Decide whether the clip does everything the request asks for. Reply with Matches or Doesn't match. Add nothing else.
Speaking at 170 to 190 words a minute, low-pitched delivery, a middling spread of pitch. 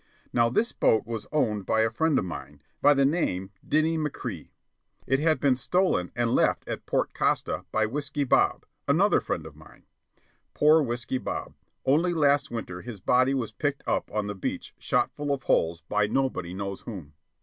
Doesn't match